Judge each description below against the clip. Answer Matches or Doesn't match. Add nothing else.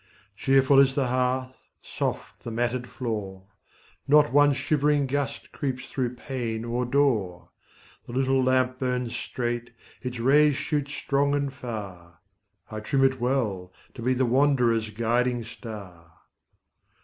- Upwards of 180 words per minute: Doesn't match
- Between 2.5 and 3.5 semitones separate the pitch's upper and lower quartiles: Matches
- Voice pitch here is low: Matches